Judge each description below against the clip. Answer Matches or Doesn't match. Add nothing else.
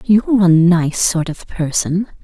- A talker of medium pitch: Matches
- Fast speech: Doesn't match